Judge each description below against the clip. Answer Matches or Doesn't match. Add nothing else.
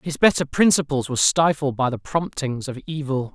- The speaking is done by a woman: Doesn't match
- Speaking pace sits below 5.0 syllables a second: Doesn't match